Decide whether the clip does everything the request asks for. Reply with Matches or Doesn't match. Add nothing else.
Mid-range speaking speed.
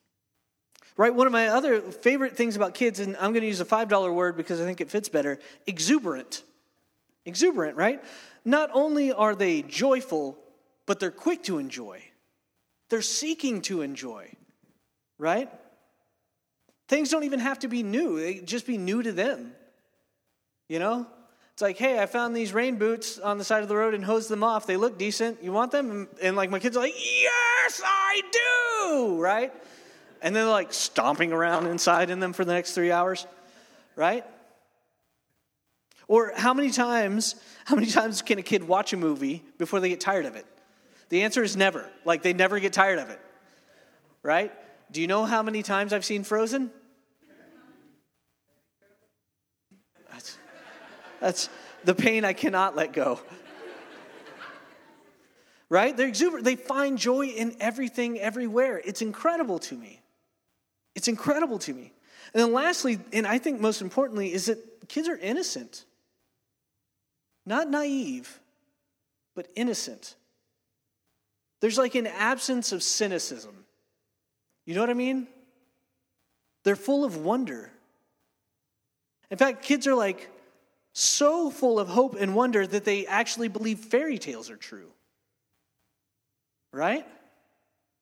Matches